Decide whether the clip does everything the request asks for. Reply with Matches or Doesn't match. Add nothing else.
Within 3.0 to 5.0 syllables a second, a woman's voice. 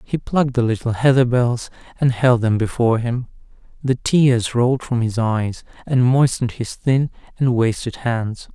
Doesn't match